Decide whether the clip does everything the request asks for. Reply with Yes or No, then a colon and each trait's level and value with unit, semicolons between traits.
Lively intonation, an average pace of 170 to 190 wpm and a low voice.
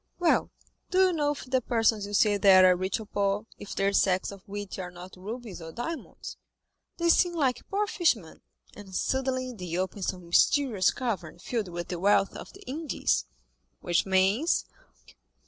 No: wide, 5.7 semitones; average, 175 wpm; high, 205 Hz